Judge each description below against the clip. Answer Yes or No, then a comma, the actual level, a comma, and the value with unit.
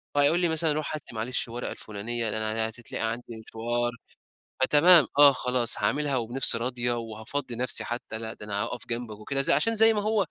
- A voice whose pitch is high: No, low, 120 Hz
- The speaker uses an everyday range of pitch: Yes, average, 4.2 semitones